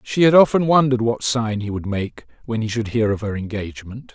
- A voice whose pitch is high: No, low, 115 Hz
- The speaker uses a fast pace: Yes, fast, 230 wpm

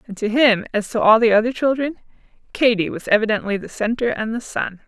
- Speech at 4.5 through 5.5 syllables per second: No, 5.9 syllables/s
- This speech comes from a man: No, female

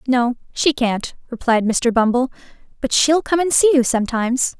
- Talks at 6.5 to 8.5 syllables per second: No, 5.0 syllables/s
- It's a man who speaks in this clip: No, female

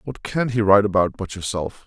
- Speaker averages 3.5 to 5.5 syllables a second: No, 6.0 syllables/s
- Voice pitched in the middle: No, low, 105 Hz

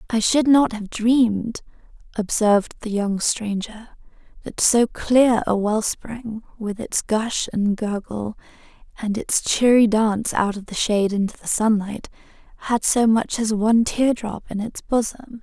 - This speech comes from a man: No, female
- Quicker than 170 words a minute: No, average, 160 wpm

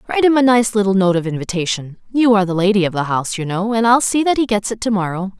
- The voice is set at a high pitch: Yes, high, 205 Hz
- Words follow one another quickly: Yes, fast, 255 wpm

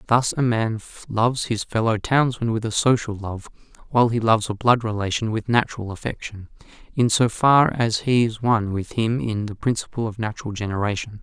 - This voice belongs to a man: Yes, male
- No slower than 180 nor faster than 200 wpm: Yes, average, 185 wpm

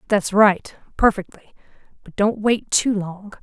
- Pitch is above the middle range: Yes, high, 205 Hz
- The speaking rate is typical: No, slow, 125 wpm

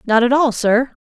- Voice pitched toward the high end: Yes, high, 245 Hz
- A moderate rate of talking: No, fast, 235 wpm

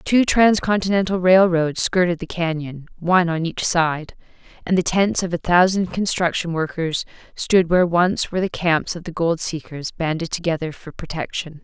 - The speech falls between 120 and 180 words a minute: Yes, average, 165 wpm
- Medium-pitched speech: Yes, medium, 170 Hz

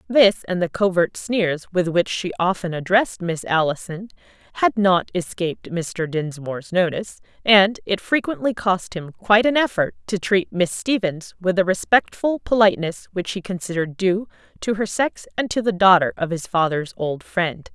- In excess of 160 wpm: Yes, average, 170 wpm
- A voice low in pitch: No, high, 190 Hz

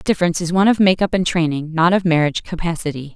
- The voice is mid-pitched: Yes, medium, 170 Hz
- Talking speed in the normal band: No, fast, 230 wpm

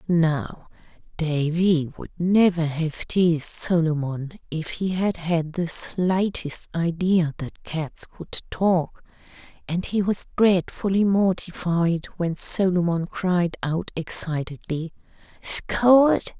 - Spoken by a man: No, female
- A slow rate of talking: Yes, slow, 105 wpm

